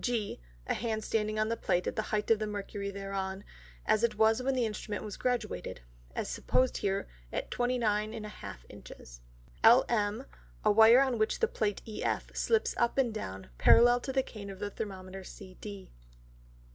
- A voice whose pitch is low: No, high, 215 Hz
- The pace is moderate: Yes, average, 170 wpm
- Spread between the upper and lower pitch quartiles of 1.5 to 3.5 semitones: Yes, average, 2.8 semitones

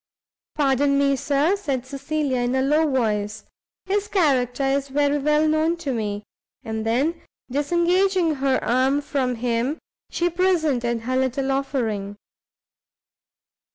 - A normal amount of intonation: Yes, average, 3.8 semitones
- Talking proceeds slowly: Yes, slow, 125 wpm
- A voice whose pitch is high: Yes, very high, 275 Hz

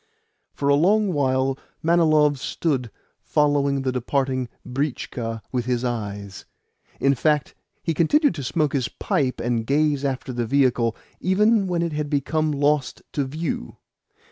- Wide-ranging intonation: No, average, 3.4 semitones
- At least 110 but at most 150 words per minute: Yes, average, 145 wpm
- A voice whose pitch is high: No, medium, 140 Hz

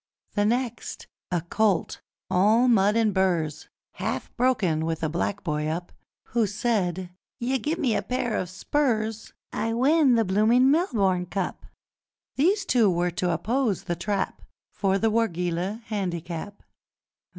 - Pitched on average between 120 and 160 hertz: No, high, 205 Hz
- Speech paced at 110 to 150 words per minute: Yes, slow, 135 wpm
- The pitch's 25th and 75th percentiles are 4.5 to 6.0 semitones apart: Yes, average, 5.0 semitones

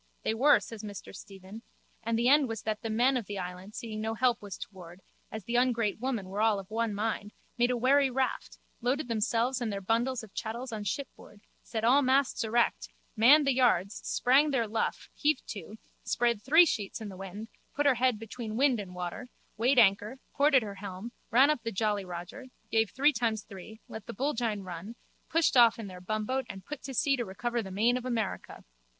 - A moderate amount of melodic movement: Yes, average, 3.7 semitones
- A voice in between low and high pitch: No, high, 225 Hz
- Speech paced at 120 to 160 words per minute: No, fast, 205 wpm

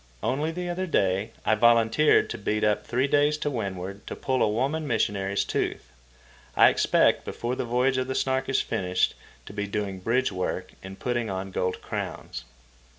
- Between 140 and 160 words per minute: No, average, 180 wpm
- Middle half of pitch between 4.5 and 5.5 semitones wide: Yes, average, 5.1 semitones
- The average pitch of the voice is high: No, low, 115 Hz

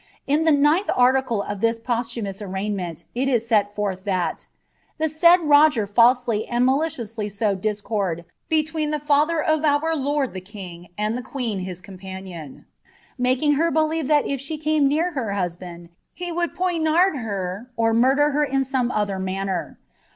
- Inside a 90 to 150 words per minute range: Yes, average, 145 wpm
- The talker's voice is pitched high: Yes, high, 240 Hz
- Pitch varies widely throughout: Yes, wide, 6.9 semitones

